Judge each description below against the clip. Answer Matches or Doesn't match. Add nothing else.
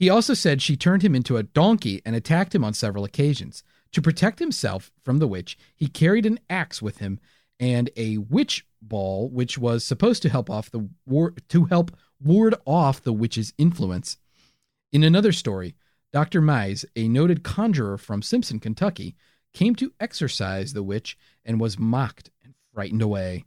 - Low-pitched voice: Matches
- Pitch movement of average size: Doesn't match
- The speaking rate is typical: Matches